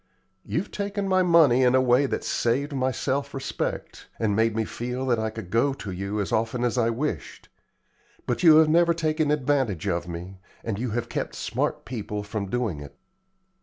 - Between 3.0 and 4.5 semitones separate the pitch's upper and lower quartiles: No, average, 5.0 semitones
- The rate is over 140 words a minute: Yes, average, 195 wpm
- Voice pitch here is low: Yes, low, 125 Hz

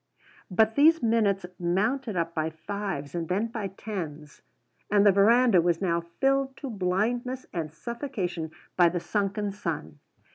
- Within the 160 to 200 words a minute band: No, average, 145 wpm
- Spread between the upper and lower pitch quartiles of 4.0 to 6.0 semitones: Yes, average, 5.1 semitones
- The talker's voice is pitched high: Yes, high, 195 Hz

